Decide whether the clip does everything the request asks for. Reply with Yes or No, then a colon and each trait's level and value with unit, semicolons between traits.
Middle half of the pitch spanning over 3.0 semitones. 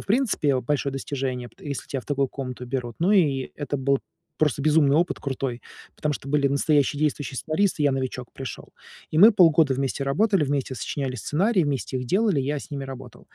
No: average, 2.7 semitones